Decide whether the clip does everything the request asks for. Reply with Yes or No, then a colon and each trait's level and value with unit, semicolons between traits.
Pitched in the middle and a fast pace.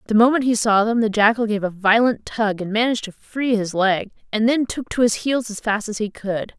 No: high, 220 Hz; fast, 255 wpm